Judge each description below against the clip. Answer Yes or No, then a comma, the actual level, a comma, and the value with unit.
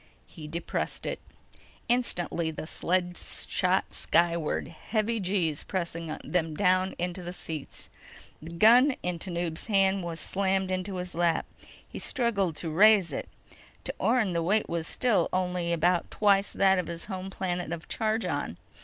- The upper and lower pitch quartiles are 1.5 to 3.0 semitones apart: Yes, narrow, 2.6 semitones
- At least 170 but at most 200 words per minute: No, average, 150 wpm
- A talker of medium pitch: Yes, medium, 180 Hz